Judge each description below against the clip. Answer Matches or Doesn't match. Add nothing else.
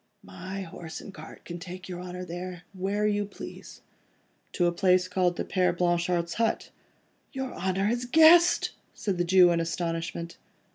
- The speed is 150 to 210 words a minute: Matches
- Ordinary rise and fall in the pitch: Doesn't match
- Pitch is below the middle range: Doesn't match